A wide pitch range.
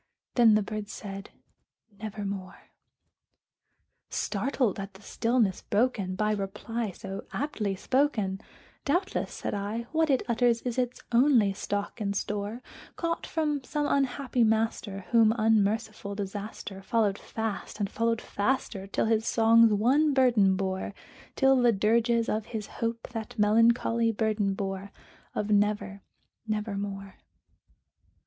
No: average, 2.8 semitones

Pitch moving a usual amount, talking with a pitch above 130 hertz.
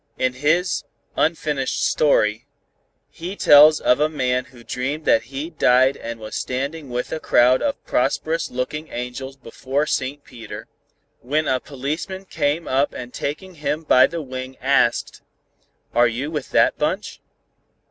Yes: average, 3.4 semitones; medium, 140 Hz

